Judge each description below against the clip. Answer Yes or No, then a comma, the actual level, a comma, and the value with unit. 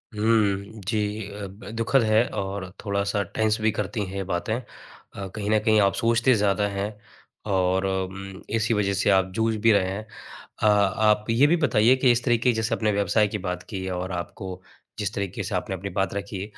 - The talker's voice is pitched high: No, low, 105 Hz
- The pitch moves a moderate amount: No, narrow, 2.2 semitones